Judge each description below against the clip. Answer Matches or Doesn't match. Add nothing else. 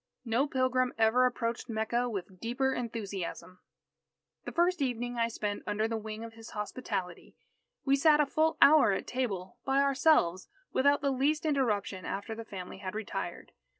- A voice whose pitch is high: Matches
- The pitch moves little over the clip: Doesn't match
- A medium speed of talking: Matches